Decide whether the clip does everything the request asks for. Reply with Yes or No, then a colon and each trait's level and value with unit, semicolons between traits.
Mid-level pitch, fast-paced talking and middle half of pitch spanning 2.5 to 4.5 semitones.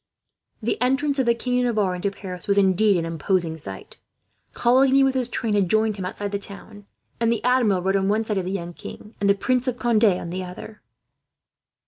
No: high, 205 Hz; fast, 215 wpm; average, 4.2 semitones